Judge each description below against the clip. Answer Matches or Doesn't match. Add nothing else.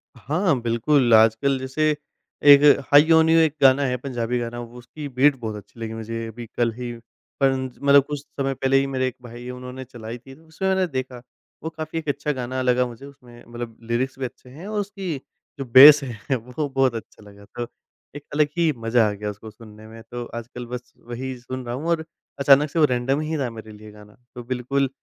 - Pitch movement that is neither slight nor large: Matches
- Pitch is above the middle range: Doesn't match